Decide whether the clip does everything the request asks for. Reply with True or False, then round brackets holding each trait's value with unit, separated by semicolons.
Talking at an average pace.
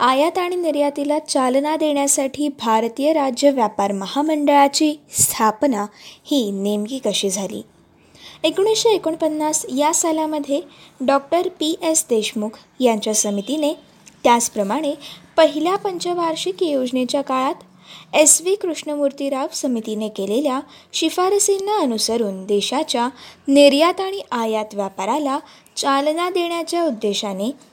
True (95 wpm)